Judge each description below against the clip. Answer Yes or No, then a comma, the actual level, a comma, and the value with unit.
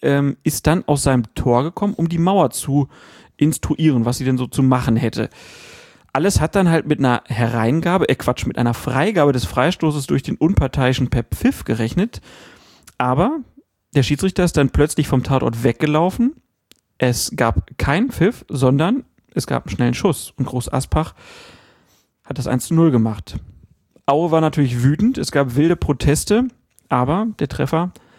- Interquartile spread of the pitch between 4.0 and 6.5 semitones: Yes, average, 4.7 semitones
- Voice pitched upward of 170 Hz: No, medium, 140 Hz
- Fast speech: No, average, 165 wpm